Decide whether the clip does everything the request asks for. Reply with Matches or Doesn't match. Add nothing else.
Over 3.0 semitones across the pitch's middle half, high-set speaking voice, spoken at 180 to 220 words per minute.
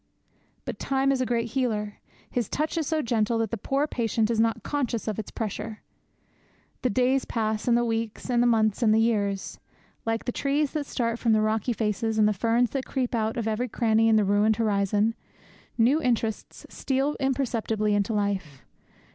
Doesn't match